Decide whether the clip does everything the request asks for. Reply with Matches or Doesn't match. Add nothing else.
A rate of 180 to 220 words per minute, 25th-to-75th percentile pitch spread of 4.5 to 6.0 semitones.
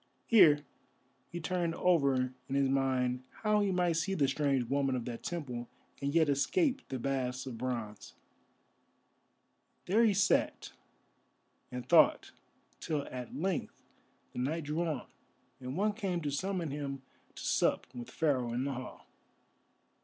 Doesn't match